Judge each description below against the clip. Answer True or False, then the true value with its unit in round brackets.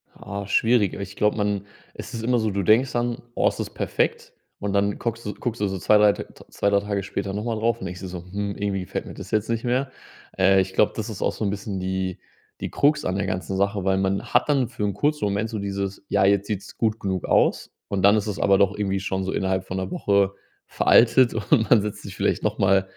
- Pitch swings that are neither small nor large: False (2.2 semitones)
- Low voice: True (100 Hz)